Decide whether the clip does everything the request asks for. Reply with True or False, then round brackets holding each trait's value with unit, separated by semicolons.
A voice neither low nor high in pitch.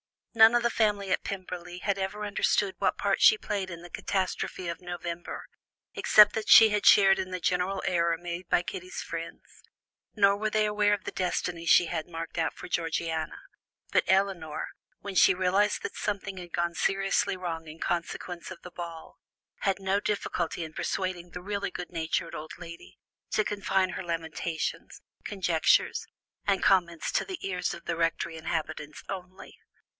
True (180 Hz)